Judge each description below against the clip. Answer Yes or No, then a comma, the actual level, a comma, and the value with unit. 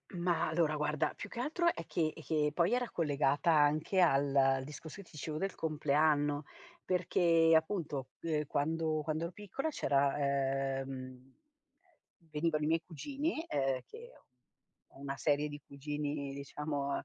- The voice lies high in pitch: No, medium, 150 Hz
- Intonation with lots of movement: No, average, 2.9 semitones